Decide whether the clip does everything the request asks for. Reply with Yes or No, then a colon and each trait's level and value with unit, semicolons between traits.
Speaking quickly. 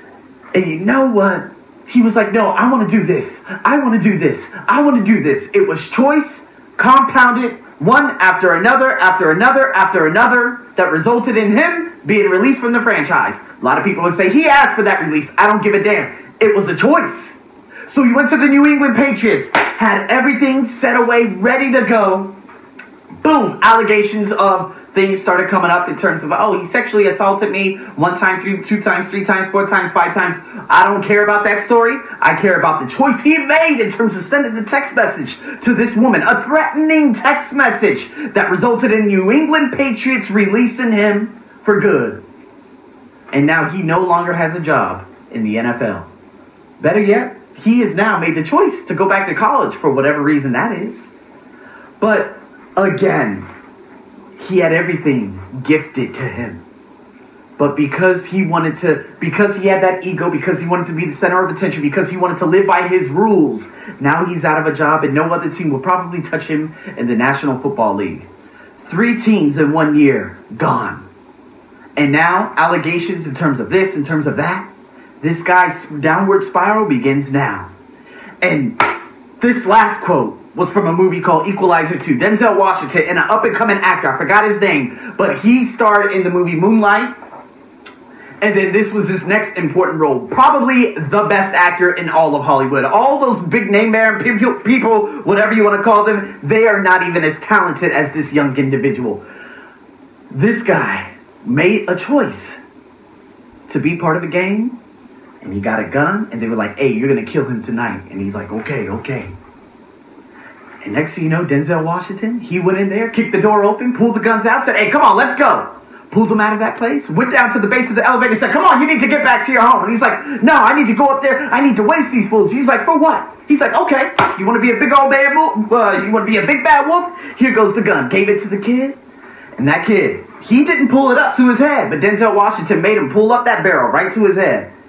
Yes: fast, 210 wpm